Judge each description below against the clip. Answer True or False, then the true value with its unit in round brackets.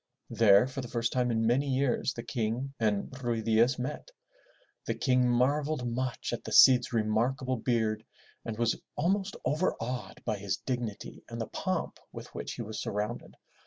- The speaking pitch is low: True (120 Hz)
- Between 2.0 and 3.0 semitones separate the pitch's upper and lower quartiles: True (2.6 semitones)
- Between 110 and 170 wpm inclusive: True (165 wpm)